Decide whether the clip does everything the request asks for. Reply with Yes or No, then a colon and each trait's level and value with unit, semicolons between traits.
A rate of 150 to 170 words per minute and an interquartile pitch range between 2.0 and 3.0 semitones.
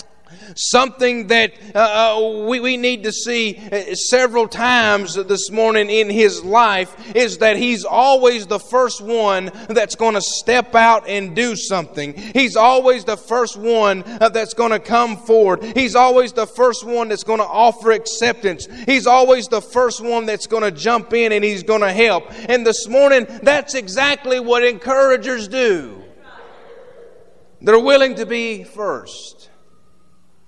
Yes: average, 155 wpm; average, 2.7 semitones